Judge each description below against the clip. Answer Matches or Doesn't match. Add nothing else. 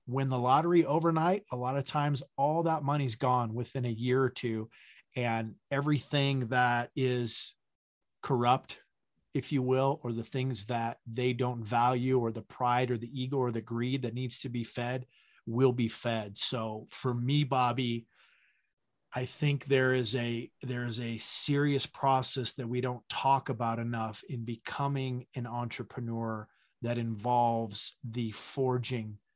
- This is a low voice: Matches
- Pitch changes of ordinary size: Doesn't match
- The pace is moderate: Matches